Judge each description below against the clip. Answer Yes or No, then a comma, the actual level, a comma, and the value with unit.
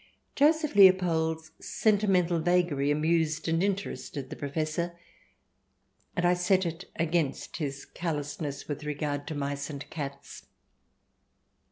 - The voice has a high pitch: No, medium, 160 Hz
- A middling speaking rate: No, slow, 120 wpm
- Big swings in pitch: No, average, 3.4 semitones